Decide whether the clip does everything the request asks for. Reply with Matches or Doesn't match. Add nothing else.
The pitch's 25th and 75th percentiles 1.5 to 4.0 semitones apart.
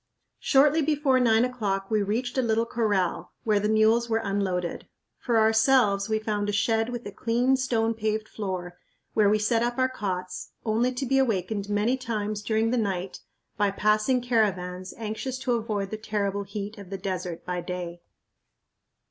Matches